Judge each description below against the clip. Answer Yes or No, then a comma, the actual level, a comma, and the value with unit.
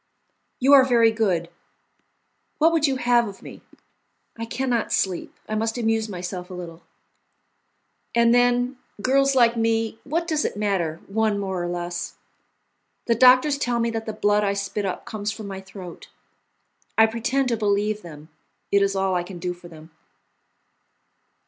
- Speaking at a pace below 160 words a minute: No, average, 170 wpm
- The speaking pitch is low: No, high, 220 Hz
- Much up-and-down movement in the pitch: No, average, 4.1 semitones